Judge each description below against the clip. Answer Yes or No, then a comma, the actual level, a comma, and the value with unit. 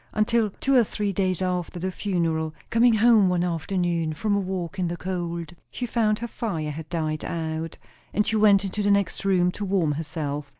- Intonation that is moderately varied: Yes, average, 3.9 semitones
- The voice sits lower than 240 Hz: Yes, medium, 185 Hz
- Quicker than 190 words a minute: Yes, average, 200 wpm